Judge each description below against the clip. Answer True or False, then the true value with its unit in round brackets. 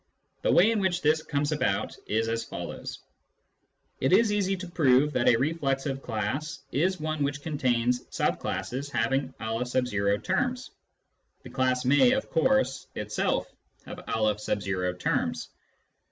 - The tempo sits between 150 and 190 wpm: False (140 wpm)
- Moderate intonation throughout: False (5.8 semitones)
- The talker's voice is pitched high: False (135 Hz)